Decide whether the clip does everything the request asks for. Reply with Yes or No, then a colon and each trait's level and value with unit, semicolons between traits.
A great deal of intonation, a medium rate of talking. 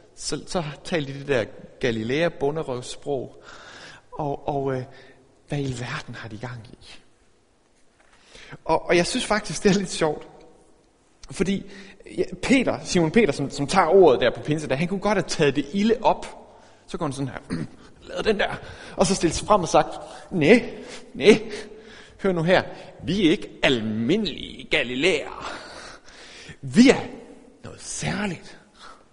Yes: wide, 6.5 semitones; average, 160 wpm